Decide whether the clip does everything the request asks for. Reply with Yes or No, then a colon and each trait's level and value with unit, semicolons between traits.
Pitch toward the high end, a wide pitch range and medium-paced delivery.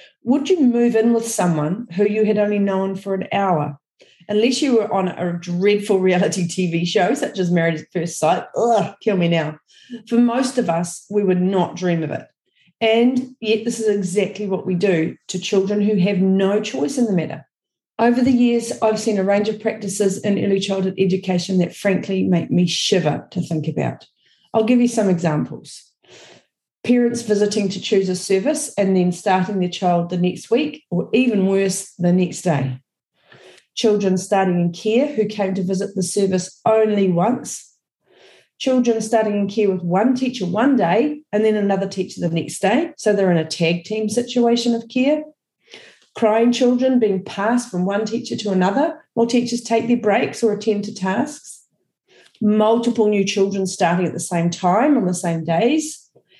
No: high, 200 Hz; average, 4.0 semitones; average, 185 wpm